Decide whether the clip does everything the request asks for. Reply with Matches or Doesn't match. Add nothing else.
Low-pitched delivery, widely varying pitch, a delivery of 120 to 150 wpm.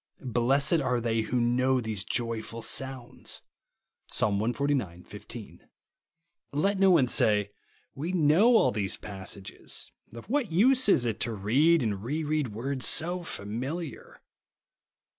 Matches